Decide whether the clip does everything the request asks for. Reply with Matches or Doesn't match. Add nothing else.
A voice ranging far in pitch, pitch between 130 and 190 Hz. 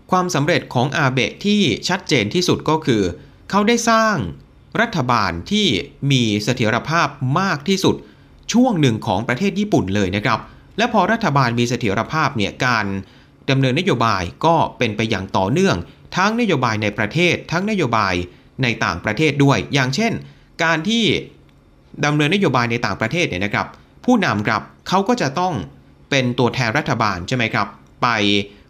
Matches